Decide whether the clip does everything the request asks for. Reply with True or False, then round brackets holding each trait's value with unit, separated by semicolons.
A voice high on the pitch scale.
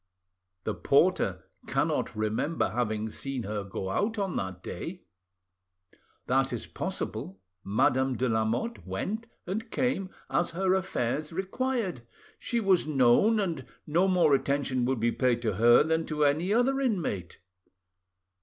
False (145 Hz)